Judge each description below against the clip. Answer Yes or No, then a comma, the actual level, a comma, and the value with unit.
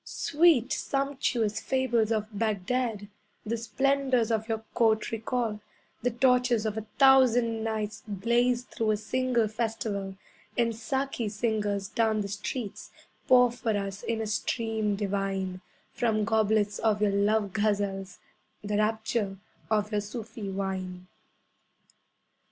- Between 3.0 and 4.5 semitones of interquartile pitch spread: No, narrow, 2.6 semitones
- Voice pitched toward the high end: Yes, high, 220 Hz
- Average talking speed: No, slow, 125 wpm